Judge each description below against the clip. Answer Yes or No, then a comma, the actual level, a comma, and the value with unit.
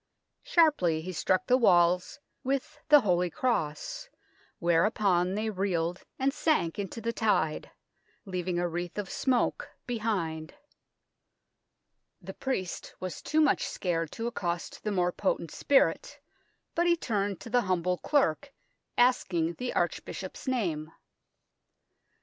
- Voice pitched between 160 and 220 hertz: Yes, high, 190 Hz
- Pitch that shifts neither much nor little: No, wide, 6.2 semitones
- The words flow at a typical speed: No, slow, 125 wpm